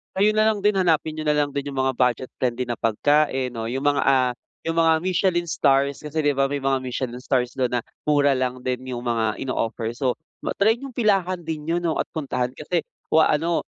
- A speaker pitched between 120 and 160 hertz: Yes, medium, 140 Hz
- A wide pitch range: No, average, 4.4 semitones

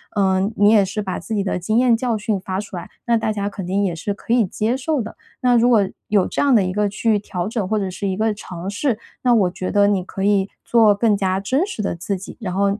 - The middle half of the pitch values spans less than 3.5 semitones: Yes, average, 2.7 semitones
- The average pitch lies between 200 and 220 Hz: Yes, high, 205 Hz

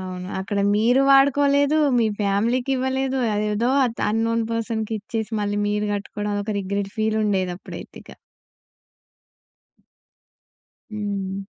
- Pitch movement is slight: No, average, 3.1 semitones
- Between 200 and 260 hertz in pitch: Yes, high, 215 Hz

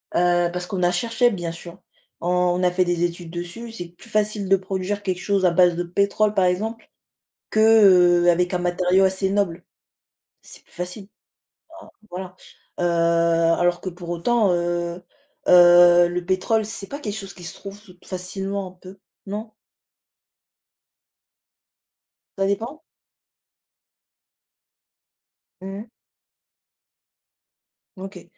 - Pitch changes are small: Yes, narrow, 2.3 semitones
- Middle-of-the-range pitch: Yes, medium, 180 Hz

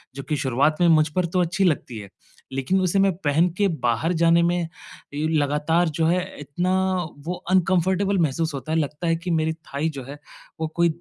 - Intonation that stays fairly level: No, average, 3.2 semitones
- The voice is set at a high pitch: No, medium, 160 Hz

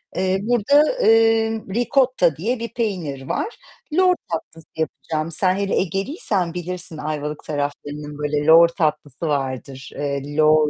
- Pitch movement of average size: No, wide, 6.9 semitones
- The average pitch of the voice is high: No, medium, 165 Hz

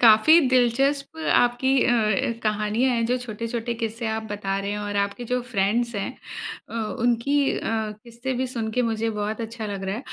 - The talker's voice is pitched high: Yes, high, 230 Hz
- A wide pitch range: No, narrow, 2.5 semitones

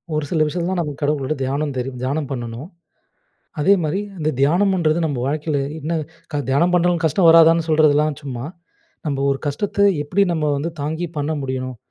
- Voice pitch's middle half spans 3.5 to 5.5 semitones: No, average, 3.1 semitones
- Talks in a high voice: No, medium, 150 Hz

